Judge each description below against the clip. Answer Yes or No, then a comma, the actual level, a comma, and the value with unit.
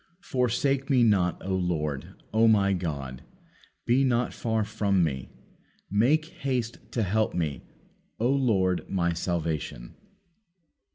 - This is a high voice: No, low, 100 Hz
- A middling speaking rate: No, slow, 120 wpm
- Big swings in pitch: Yes, wide, 5.8 semitones